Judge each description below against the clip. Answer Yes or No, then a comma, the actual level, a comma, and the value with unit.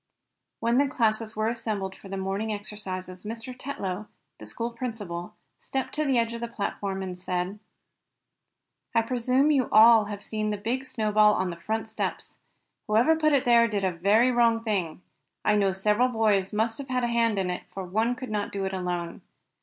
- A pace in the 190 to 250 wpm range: Yes, average, 195 wpm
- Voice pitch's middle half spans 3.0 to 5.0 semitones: Yes, average, 3.3 semitones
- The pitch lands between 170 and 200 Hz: No, high, 215 Hz